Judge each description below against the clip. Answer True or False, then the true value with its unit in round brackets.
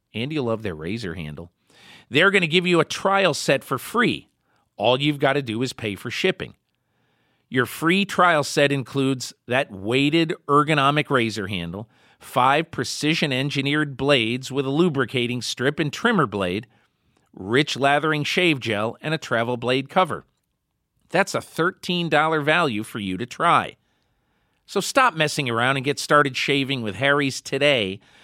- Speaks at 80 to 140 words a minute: False (155 wpm)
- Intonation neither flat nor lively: True (4.4 semitones)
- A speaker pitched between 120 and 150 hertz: True (140 Hz)